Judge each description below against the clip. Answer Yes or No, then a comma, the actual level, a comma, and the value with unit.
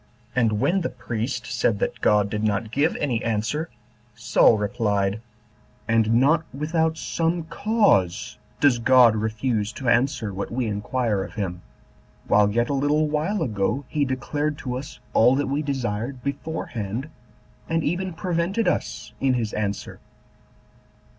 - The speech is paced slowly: No, average, 145 wpm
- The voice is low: Yes, low, 125 Hz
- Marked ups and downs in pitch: Yes, wide, 5.7 semitones